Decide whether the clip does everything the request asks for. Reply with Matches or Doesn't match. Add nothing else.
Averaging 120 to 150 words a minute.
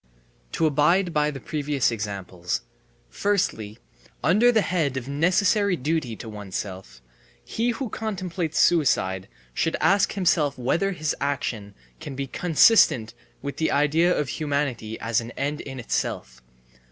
Matches